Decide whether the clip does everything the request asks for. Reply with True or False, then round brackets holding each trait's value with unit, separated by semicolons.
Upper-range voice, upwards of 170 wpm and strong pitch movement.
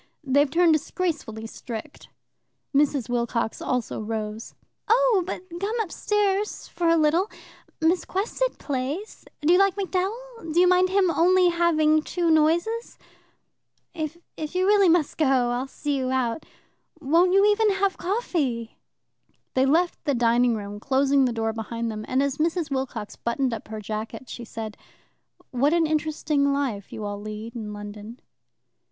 False (295 Hz; 150 wpm; 7.1 semitones)